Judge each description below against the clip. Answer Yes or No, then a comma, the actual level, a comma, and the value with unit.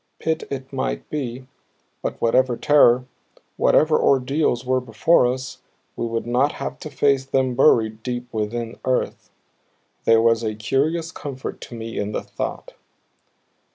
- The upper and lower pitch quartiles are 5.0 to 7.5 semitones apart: No, average, 2.9 semitones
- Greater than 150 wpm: No, average, 145 wpm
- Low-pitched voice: Yes, low, 125 Hz